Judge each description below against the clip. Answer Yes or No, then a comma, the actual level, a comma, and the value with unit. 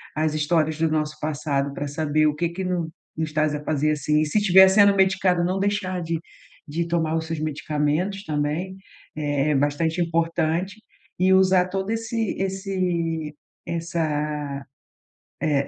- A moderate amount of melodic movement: Yes, average, 3.5 semitones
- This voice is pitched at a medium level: Yes, medium, 165 Hz